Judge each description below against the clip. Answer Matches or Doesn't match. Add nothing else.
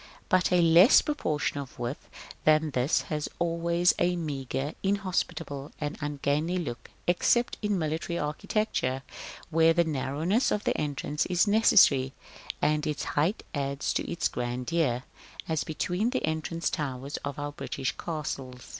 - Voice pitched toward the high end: Doesn't match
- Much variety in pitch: Doesn't match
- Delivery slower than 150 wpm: Matches